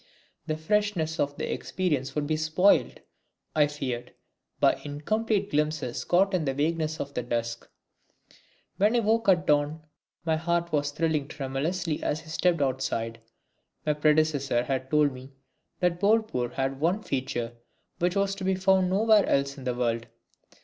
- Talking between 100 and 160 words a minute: Yes, average, 155 wpm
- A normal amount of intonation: Yes, average, 5.0 semitones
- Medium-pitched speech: Yes, medium, 155 Hz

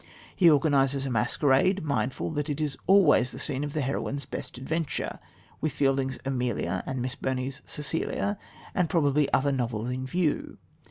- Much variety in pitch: No, average, 2.8 semitones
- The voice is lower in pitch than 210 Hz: Yes, medium, 140 Hz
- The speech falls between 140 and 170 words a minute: Yes, average, 160 wpm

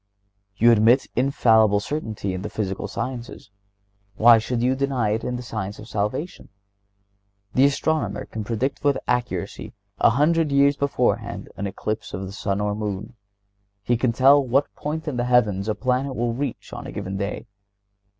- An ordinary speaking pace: Yes, average, 170 wpm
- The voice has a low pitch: Yes, low, 120 Hz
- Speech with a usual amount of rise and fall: Yes, average, 4.3 semitones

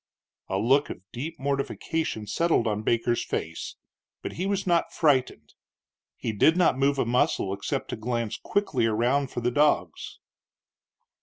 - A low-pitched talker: Yes, low, 130 Hz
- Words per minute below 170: Yes, average, 150 wpm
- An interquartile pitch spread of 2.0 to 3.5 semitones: No, average, 4.9 semitones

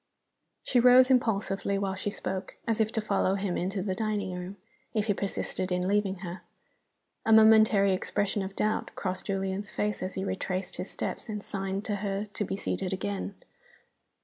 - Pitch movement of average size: No, narrow, 1.9 semitones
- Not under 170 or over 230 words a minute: Yes, average, 180 wpm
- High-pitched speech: Yes, high, 195 Hz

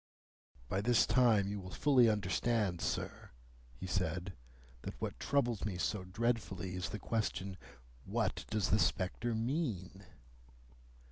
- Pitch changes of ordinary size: Yes, average, 4.1 semitones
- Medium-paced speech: No, slow, 130 wpm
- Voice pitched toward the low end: Yes, low, 100 Hz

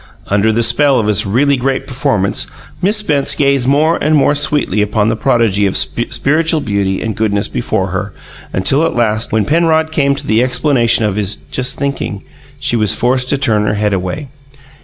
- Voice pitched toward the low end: Yes, low, 125 Hz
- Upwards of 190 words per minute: No, average, 185 wpm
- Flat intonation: No, average, 5.0 semitones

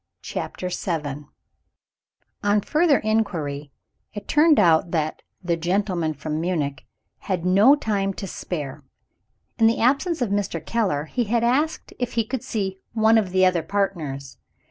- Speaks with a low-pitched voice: No, high, 195 Hz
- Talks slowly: No, average, 145 wpm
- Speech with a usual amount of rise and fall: No, wide, 5.8 semitones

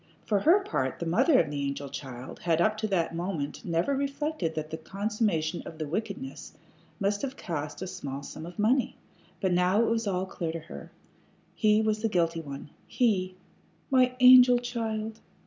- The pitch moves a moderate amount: No, wide, 5.8 semitones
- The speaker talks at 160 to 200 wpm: Yes, average, 180 wpm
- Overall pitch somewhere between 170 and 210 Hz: Yes, high, 190 Hz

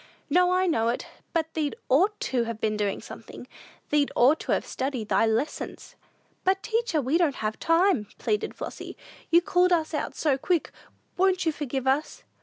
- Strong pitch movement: Yes, wide, 6.5 semitones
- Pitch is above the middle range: Yes, very high, 300 Hz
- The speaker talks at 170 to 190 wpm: Yes, average, 180 wpm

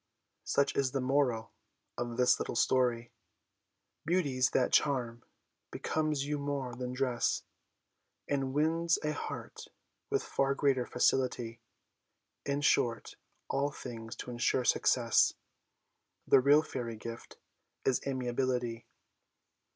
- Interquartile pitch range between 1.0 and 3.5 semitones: Yes, average, 2.7 semitones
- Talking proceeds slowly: Yes, slow, 115 wpm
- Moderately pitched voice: No, low, 130 Hz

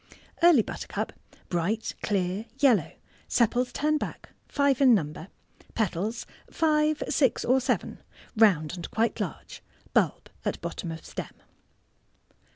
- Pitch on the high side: Yes, high, 230 Hz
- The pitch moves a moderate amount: No, wide, 6.7 semitones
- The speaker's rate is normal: No, slow, 120 wpm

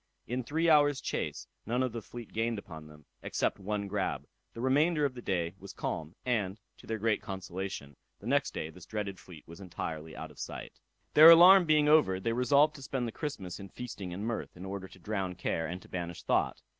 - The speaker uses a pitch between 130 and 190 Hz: No, low, 105 Hz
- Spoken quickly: Yes, fast, 215 wpm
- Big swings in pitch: Yes, wide, 6.0 semitones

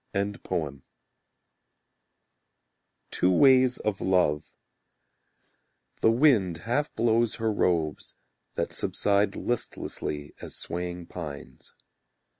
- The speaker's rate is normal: No, slow, 75 wpm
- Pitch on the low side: Yes, low, 100 Hz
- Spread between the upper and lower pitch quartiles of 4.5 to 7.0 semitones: Yes, wide, 5.5 semitones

